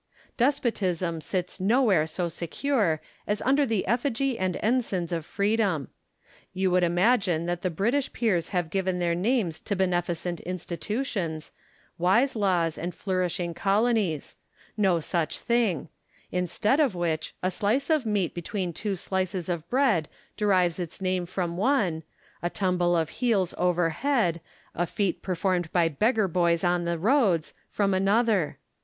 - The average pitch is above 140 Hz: Yes, medium, 185 Hz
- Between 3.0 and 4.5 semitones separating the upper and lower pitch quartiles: Yes, average, 4.0 semitones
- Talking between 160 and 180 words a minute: No, average, 145 wpm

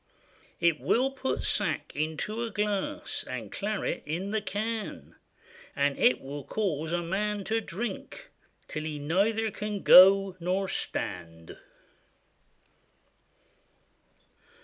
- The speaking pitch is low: No, high, 195 Hz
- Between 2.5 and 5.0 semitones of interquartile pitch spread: No, wide, 5.5 semitones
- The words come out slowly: Yes, slow, 110 wpm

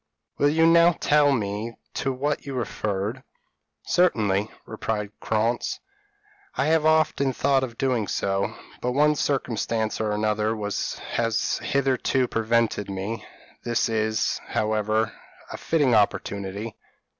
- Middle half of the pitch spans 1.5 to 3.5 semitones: No, average, 4.3 semitones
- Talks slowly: Yes, slow, 115 wpm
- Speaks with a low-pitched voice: Yes, low, 115 Hz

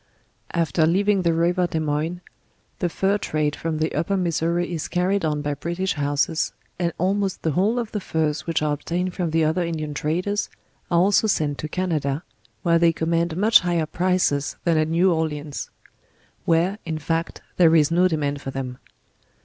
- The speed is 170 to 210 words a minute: Yes, average, 180 wpm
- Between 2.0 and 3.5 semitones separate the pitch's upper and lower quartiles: Yes, average, 2.8 semitones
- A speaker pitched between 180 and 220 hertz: No, medium, 165 Hz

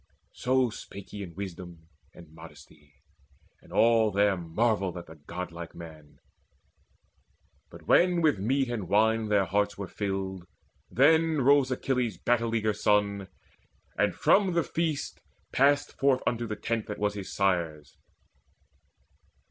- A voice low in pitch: Yes, low, 105 Hz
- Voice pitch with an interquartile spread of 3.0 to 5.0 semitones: No, wide, 5.4 semitones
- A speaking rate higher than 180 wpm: No, average, 140 wpm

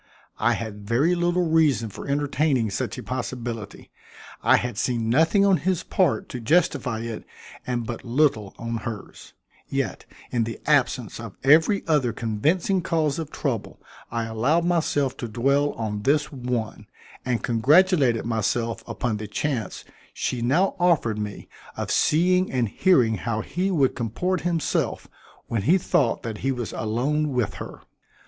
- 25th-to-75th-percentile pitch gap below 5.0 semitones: No, wide, 5.6 semitones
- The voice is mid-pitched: No, low, 125 Hz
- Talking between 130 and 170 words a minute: Yes, average, 155 wpm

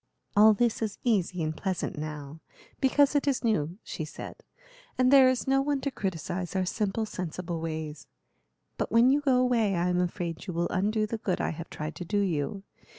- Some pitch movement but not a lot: No, wide, 6.0 semitones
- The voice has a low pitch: No, high, 195 Hz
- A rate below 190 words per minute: No, average, 200 wpm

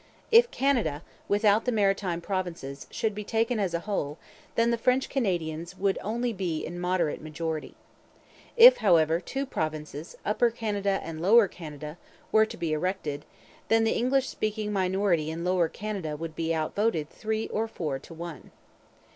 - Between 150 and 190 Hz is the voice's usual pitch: Yes, medium, 185 Hz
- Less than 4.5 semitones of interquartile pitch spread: No, wide, 5.4 semitones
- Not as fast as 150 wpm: No, average, 165 wpm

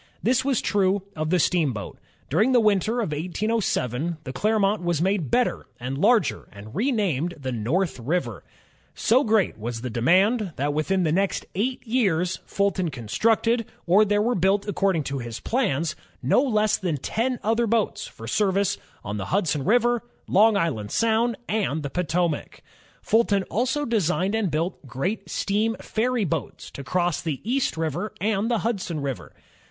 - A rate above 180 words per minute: No, average, 165 wpm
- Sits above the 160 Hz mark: Yes, high, 190 Hz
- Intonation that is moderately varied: No, wide, 6.4 semitones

